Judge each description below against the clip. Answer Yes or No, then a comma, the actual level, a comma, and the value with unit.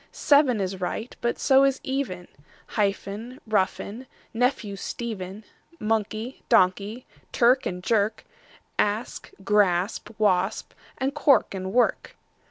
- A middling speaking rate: No, slow, 110 wpm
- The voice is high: Yes, high, 215 Hz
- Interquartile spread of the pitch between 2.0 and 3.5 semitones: No, average, 4.2 semitones